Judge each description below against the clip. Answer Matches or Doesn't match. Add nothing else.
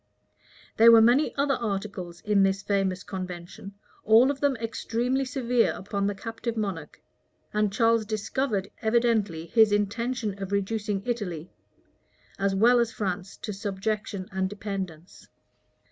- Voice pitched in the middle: Doesn't match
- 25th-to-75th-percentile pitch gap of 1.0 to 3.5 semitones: Matches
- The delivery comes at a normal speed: Doesn't match